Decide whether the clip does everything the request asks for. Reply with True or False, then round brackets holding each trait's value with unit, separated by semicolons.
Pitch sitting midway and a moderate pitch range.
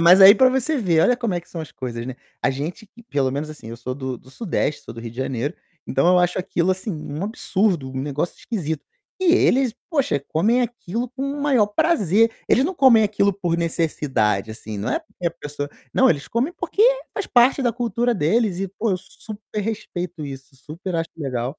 False (180 Hz; 8.4 semitones)